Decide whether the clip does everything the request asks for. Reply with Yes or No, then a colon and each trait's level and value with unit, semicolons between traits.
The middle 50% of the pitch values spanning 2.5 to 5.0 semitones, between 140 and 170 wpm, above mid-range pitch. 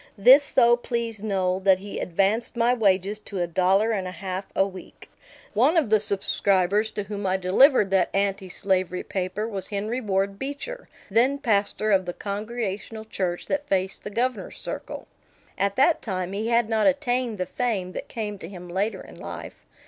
No: average, 3.5 semitones; average, 180 wpm; high, 205 Hz